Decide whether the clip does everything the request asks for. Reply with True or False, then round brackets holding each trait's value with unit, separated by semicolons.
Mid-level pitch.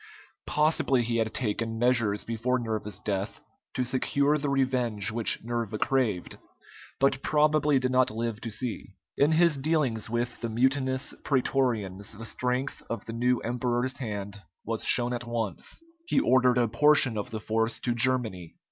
False (120 Hz)